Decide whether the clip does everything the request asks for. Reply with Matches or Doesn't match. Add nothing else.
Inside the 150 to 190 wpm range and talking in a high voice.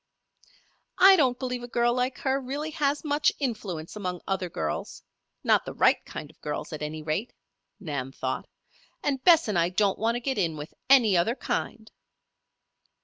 Matches